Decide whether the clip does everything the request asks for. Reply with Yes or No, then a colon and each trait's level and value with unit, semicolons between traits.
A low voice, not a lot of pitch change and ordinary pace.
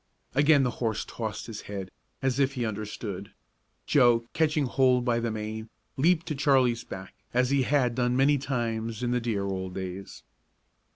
No: low, 120 Hz; average, 3.6 semitones; average, 170 wpm